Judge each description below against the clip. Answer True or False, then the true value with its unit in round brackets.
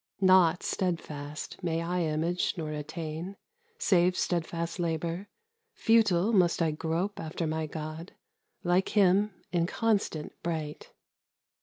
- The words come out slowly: True (110 wpm)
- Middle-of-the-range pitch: True (170 Hz)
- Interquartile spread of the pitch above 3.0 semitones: False (2.6 semitones)